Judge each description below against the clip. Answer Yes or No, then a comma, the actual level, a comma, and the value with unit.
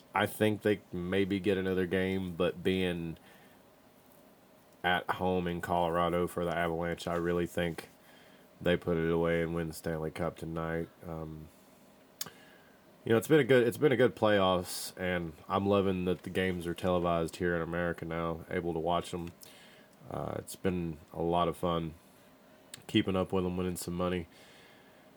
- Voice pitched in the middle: No, very low, 90 Hz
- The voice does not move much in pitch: Yes, narrow, 1.9 semitones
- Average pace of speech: Yes, average, 170 wpm